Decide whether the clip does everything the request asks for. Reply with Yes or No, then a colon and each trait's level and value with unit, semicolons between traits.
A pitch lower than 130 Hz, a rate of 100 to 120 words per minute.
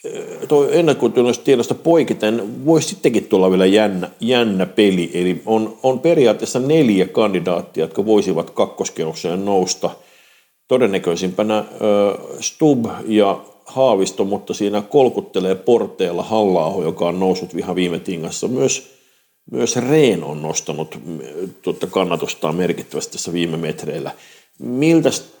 Yes: low, 105 Hz; average, 115 wpm